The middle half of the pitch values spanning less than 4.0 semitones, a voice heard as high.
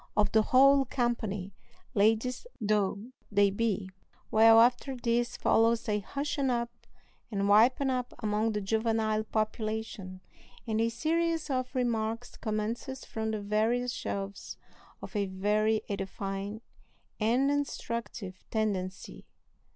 Yes: average, 2.7 semitones; high, 220 Hz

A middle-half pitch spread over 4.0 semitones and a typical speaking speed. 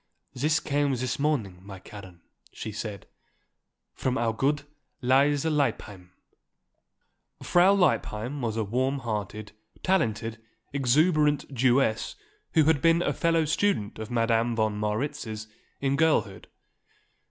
No: average, 5.2 semitones; slow, 120 wpm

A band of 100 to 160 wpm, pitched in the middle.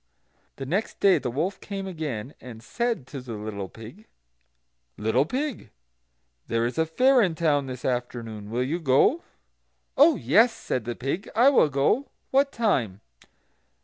Yes: average, 155 wpm; medium, 145 Hz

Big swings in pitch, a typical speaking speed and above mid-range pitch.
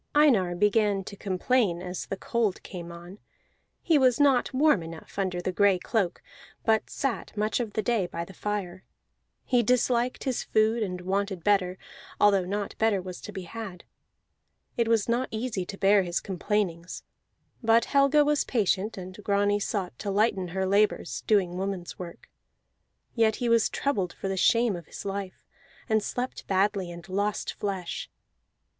No: average, 3.5 semitones; average, 165 wpm; high, 200 Hz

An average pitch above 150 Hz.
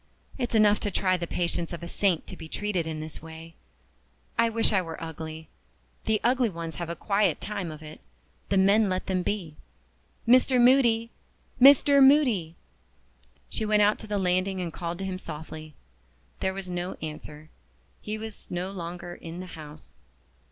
Yes: medium, 185 Hz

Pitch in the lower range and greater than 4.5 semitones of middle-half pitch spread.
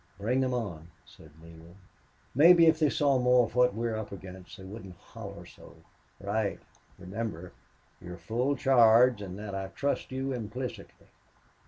Yes: low, 110 Hz; average, 5.1 semitones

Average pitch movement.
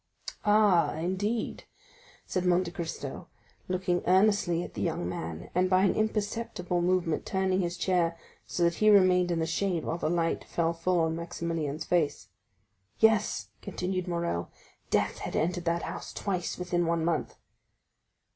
No: narrow, 1.9 semitones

